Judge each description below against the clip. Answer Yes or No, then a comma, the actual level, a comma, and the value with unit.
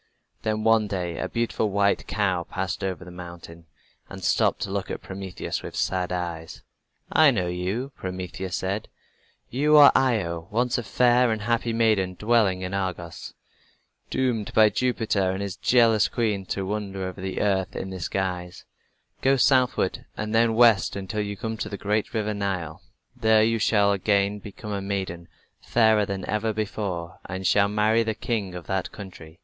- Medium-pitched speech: No, low, 100 Hz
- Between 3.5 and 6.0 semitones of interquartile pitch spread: No, average, 3.1 semitones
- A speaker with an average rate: Yes, average, 170 wpm